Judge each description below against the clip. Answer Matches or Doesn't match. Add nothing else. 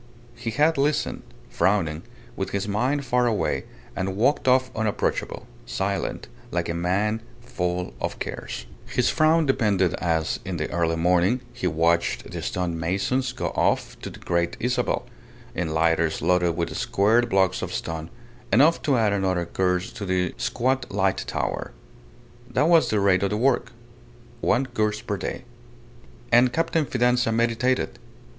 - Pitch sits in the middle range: Doesn't match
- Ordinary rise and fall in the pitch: Doesn't match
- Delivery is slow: Doesn't match